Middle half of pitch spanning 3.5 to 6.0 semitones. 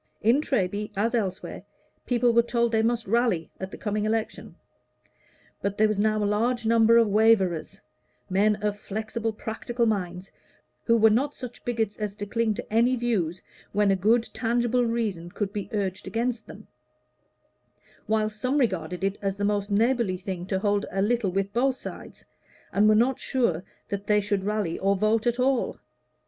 No: average, 2.7 semitones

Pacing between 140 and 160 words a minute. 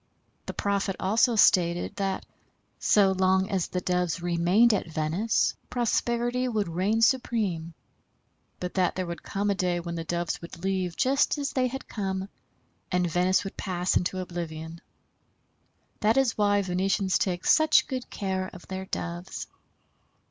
Yes: average, 150 wpm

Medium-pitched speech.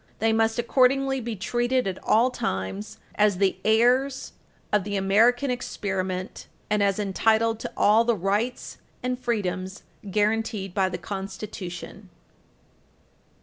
No: high, 210 Hz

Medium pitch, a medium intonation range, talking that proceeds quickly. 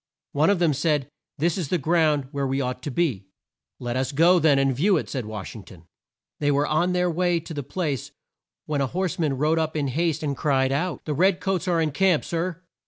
Yes: medium, 155 Hz; average, 4.0 semitones; fast, 235 wpm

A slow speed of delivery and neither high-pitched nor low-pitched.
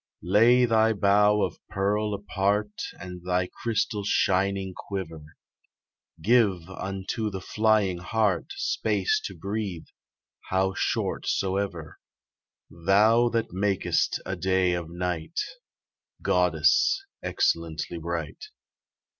No: slow, 100 wpm; very low, 95 Hz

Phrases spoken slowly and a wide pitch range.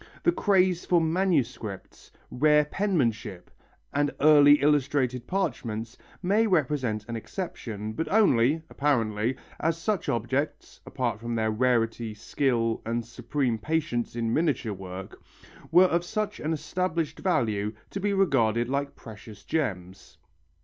Yes: slow, 130 wpm; wide, 6.2 semitones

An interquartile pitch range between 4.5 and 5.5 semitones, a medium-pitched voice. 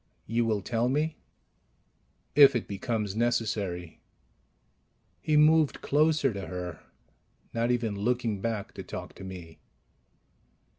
No: average, 4.9 semitones; low, 115 Hz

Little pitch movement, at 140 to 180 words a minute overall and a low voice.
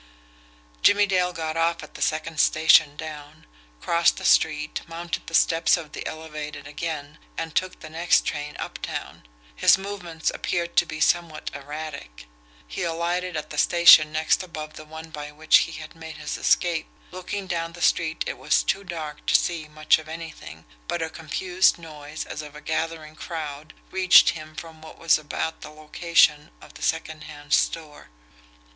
No: narrow, 1.7 semitones; average, 170 wpm; medium, 160 Hz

